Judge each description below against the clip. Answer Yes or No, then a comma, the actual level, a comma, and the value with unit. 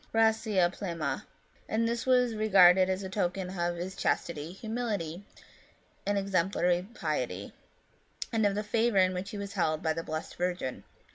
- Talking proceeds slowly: No, average, 160 wpm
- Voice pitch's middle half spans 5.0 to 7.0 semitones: No, average, 3.6 semitones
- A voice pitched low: No, high, 190 Hz